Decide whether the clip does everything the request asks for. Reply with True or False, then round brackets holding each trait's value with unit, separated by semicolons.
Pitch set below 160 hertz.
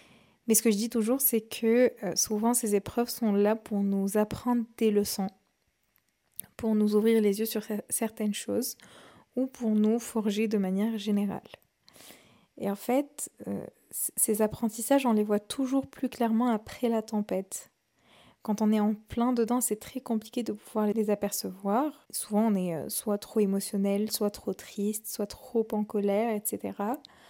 False (220 Hz)